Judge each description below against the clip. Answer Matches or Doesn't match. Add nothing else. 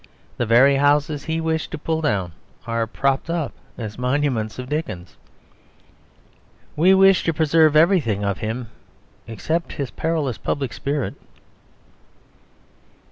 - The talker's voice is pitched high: Doesn't match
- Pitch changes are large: Matches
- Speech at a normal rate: Doesn't match